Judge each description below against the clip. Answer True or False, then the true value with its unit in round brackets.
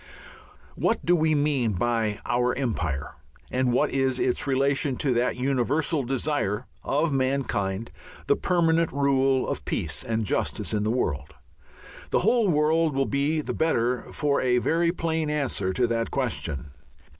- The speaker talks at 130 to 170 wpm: True (150 wpm)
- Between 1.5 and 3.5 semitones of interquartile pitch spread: False (4.3 semitones)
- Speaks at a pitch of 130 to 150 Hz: True (135 Hz)